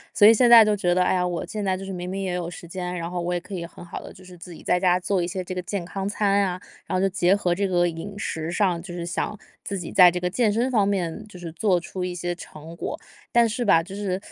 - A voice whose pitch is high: No, medium, 180 Hz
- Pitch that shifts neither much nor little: No, narrow, 2.2 semitones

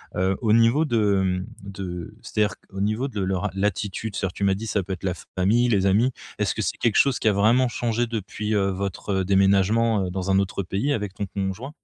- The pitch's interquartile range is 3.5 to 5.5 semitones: No, average, 2.8 semitones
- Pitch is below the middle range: Yes, low, 100 Hz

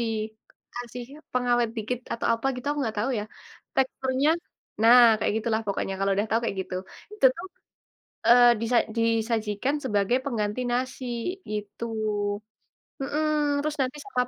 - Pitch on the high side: Yes, high, 235 Hz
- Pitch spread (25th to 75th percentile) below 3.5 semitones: Yes, average, 2.9 semitones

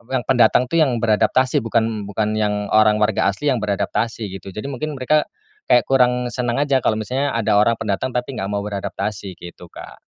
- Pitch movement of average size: Yes, average, 3.5 semitones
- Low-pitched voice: Yes, low, 115 Hz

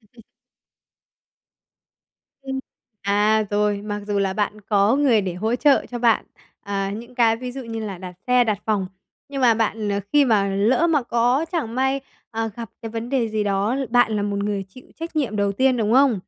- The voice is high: Yes, high, 225 Hz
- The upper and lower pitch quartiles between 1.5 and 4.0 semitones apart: Yes, average, 3.5 semitones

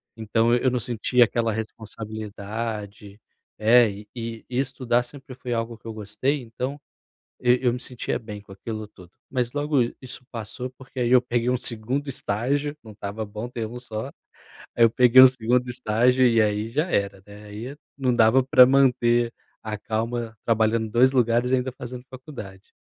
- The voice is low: Yes, low, 120 Hz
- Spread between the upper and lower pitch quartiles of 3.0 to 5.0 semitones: No, narrow, 2.5 semitones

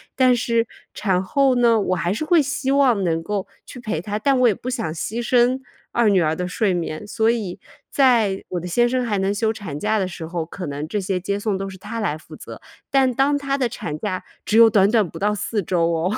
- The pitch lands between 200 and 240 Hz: Yes, high, 210 Hz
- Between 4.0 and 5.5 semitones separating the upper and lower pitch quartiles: Yes, average, 4.8 semitones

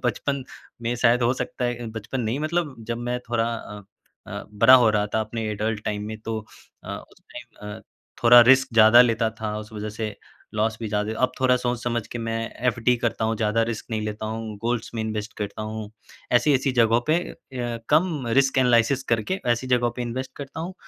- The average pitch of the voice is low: Yes, low, 115 Hz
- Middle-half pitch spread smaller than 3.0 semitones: Yes, narrow, 2.4 semitones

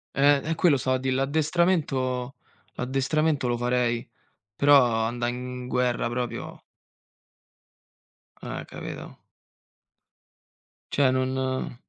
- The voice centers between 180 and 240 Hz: No, low, 130 Hz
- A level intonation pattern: Yes, narrow, 2.3 semitones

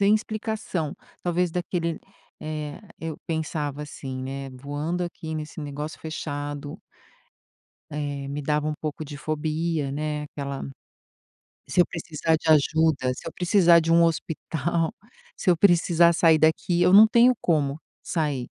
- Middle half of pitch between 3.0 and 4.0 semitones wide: No, narrow, 2.6 semitones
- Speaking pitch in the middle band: Yes, medium, 155 Hz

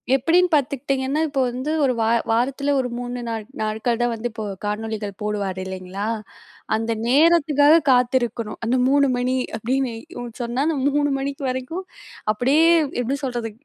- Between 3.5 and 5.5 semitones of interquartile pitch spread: Yes, average, 3.8 semitones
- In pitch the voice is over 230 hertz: Yes, very high, 250 Hz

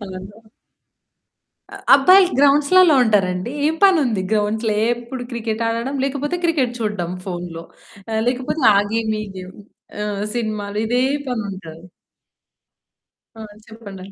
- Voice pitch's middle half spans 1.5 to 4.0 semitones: No, average, 4.9 semitones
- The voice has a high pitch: Yes, high, 225 Hz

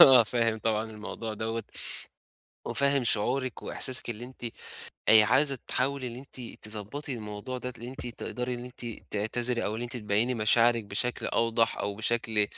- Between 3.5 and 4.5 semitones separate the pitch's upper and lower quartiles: No, narrow, 2.5 semitones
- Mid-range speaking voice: No, low, 120 Hz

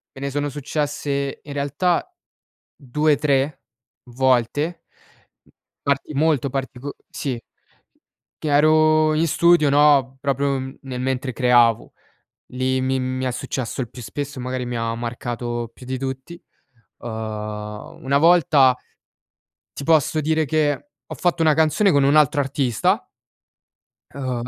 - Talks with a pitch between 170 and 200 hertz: No, medium, 140 Hz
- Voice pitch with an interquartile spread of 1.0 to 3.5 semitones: Yes, average, 2.7 semitones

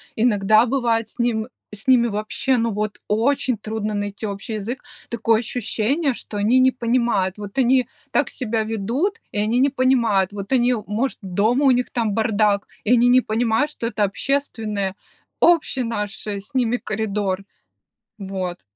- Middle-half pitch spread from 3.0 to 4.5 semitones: Yes, average, 3.3 semitones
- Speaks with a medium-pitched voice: No, high, 225 Hz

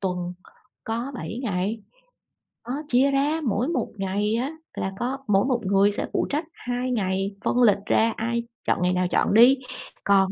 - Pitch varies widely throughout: No, average, 4.4 semitones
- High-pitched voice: Yes, high, 225 Hz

